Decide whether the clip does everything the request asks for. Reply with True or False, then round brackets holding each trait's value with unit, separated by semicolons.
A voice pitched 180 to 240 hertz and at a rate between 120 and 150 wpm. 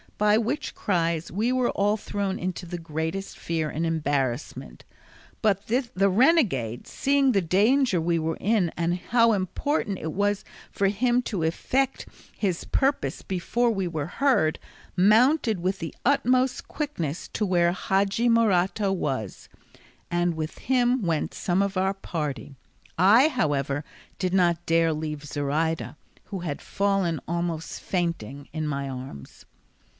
True (185 Hz; 140 wpm)